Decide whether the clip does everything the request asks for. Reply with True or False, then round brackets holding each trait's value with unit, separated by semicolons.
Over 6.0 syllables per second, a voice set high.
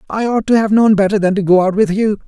True (6.4 syllables/s; 205 Hz)